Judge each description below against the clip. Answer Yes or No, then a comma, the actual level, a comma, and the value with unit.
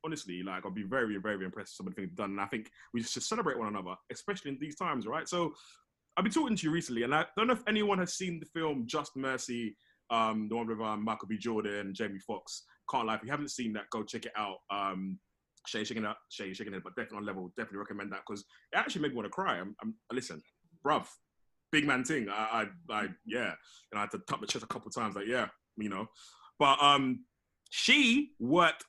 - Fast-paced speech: Yes, fast, 245 wpm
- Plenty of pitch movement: Yes, wide, 8.1 semitones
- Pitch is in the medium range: No, low, 115 Hz